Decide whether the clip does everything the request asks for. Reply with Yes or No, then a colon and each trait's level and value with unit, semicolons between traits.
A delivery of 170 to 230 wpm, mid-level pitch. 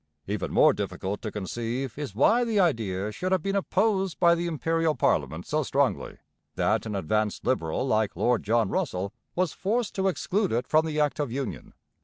Yes: average, 185 wpm; medium, 145 Hz